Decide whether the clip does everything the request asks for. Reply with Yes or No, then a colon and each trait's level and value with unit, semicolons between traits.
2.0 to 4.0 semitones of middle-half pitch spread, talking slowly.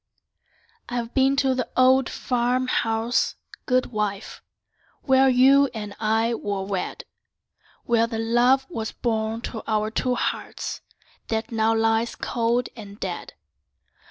Yes: narrow, 2.5 semitones; slow, 130 wpm